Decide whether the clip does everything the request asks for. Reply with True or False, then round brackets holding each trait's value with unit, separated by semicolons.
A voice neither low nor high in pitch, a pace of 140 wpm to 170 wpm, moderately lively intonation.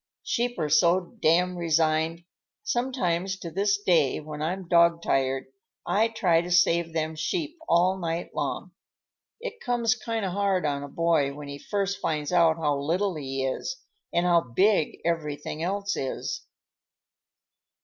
True (170 Hz; 150 wpm; 4.1 semitones)